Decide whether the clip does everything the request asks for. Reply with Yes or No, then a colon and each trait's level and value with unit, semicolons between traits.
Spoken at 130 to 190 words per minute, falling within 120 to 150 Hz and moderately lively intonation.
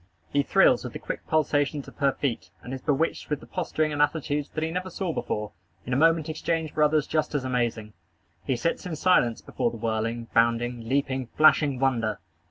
No: average, 200 wpm; medium, 140 Hz; average, 4.6 semitones